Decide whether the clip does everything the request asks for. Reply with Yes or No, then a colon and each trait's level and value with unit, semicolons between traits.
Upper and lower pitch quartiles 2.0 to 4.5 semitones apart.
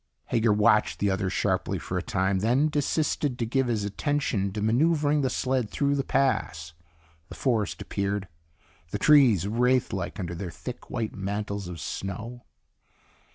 No: average, 5.1 semitones